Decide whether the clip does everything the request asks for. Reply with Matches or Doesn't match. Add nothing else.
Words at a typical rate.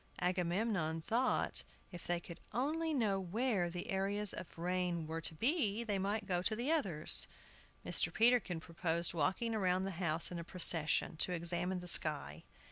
Matches